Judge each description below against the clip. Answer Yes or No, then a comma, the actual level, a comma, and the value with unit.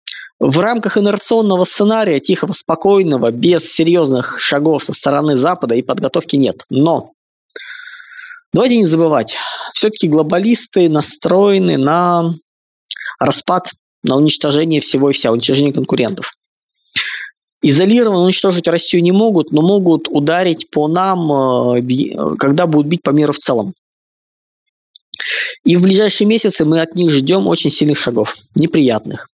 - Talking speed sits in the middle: Yes, average, 125 wpm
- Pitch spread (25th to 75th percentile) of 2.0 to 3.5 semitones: No, wide, 5.5 semitones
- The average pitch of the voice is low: No, medium, 170 Hz